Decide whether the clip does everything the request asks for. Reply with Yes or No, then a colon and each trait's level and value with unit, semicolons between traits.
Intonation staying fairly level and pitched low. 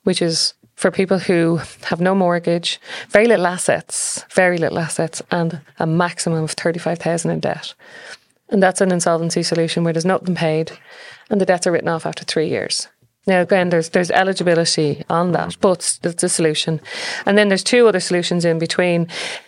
No: narrow, 2.1 semitones; medium, 175 Hz